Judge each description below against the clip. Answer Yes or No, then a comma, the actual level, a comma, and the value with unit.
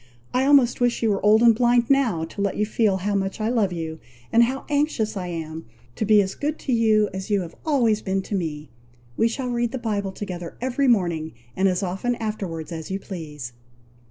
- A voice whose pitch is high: Yes, high, 210 Hz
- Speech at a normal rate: No, fast, 215 wpm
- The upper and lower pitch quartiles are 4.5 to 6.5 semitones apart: Yes, average, 4.9 semitones